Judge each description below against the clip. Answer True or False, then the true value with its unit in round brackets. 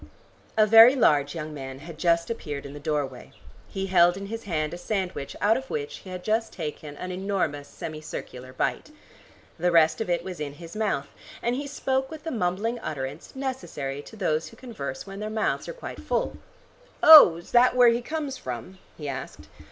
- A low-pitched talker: False (180 Hz)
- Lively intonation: True (7.3 semitones)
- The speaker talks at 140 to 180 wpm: False (200 wpm)